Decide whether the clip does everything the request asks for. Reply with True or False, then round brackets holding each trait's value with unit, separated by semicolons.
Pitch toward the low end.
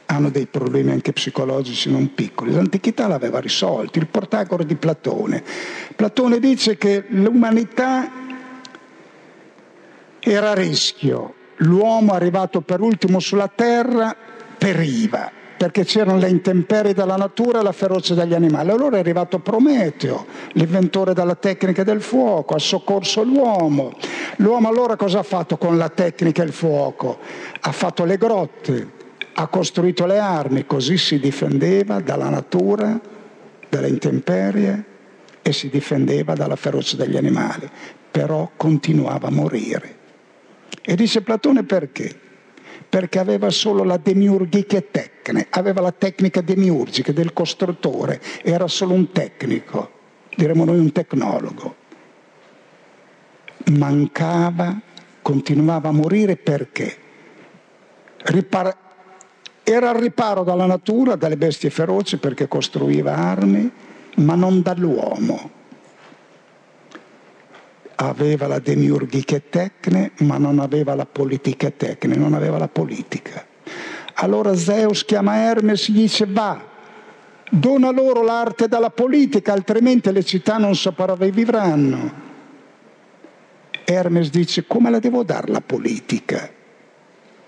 False (190 Hz)